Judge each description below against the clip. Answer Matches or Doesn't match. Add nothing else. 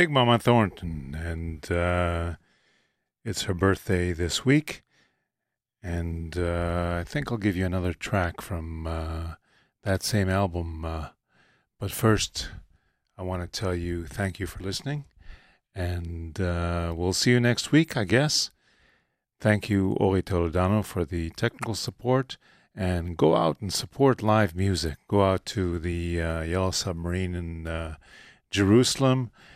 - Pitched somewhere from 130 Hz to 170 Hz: Doesn't match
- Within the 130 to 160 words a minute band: Matches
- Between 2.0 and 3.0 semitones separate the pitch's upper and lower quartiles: Doesn't match